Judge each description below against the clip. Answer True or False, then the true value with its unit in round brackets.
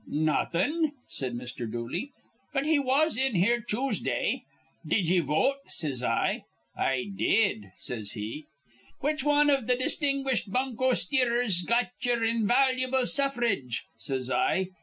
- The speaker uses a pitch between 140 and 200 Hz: False (235 Hz)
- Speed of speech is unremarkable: False (130 wpm)